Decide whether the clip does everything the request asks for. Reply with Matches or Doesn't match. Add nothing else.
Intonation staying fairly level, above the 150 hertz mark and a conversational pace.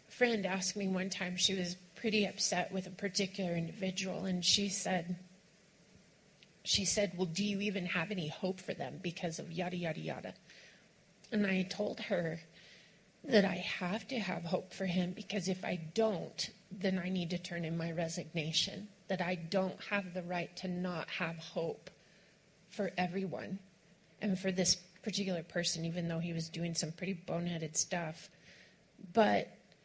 Matches